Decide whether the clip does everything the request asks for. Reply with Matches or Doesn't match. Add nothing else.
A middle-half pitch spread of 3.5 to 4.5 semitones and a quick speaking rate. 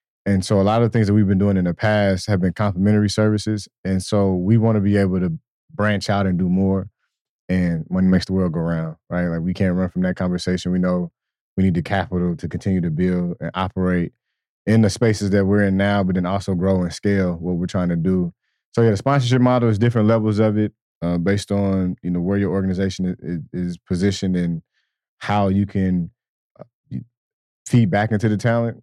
Doesn't match